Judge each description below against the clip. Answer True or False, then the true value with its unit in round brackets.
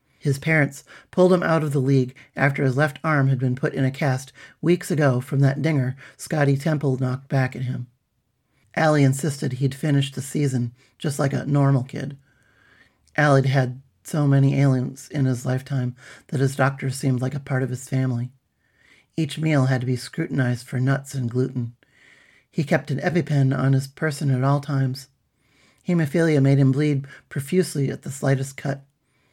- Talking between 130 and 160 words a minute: False (180 wpm)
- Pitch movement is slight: True (2.0 semitones)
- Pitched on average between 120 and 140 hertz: True (135 Hz)